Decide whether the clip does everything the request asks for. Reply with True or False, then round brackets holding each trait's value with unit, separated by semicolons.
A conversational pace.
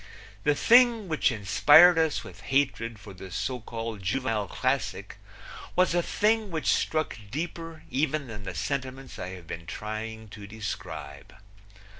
True (145 wpm)